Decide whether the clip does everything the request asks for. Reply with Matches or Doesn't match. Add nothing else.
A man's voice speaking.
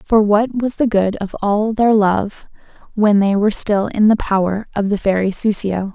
Doesn't match